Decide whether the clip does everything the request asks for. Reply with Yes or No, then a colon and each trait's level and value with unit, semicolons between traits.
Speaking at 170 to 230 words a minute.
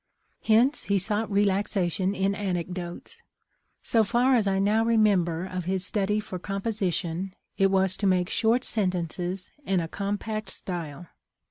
No: average, 150 wpm